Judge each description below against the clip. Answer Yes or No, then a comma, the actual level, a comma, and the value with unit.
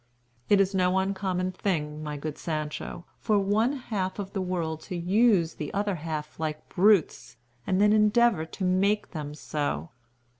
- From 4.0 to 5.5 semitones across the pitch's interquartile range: Yes, average, 4.5 semitones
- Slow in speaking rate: No, average, 160 wpm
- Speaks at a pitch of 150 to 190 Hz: Yes, medium, 185 Hz